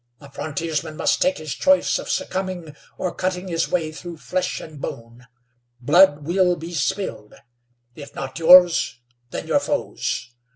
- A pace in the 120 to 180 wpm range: Yes, average, 150 wpm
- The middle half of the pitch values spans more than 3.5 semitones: Yes, average, 4.1 semitones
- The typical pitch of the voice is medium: Yes, medium, 165 Hz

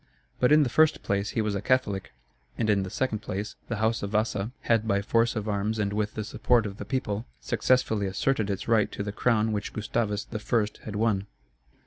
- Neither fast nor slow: No, fast, 210 wpm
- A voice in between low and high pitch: No, low, 110 Hz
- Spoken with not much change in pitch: Yes, narrow, 2.2 semitones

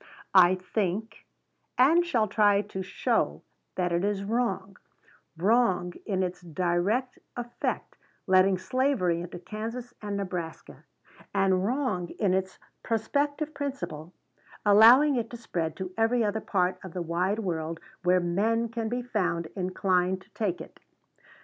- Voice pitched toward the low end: No, high, 195 Hz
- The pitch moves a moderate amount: Yes, average, 4.2 semitones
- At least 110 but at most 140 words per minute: Yes, slow, 135 wpm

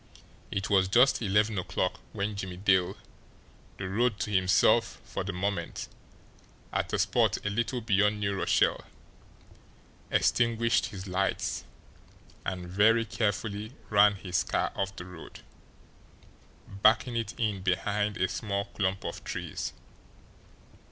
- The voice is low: Yes, low, 100 Hz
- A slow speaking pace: Yes, slow, 125 wpm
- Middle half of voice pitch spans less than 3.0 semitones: Yes, narrow, 2.5 semitones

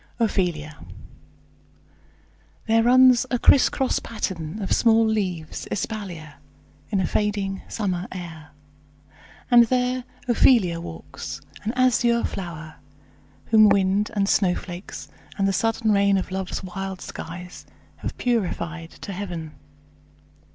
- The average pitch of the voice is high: Yes, high, 195 Hz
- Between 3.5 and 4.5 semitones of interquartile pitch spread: Yes, average, 4.2 semitones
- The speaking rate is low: Yes, slow, 110 wpm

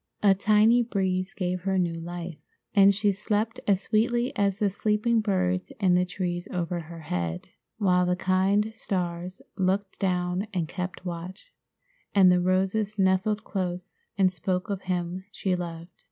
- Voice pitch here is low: No, medium, 185 Hz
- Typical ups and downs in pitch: No, narrow, 2.2 semitones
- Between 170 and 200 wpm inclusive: No, average, 155 wpm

